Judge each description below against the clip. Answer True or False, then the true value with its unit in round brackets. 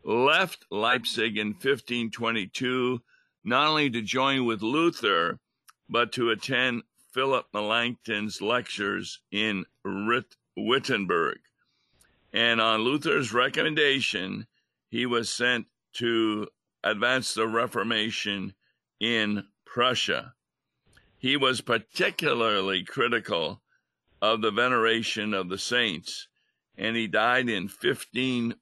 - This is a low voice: True (115 Hz)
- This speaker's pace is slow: True (95 wpm)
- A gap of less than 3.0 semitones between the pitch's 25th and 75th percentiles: True (2.4 semitones)